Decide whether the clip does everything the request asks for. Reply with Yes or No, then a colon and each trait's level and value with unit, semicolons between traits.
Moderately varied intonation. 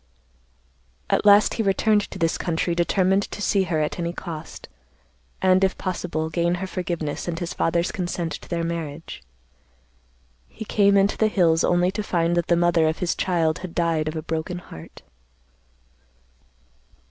No: narrow, 2.3 semitones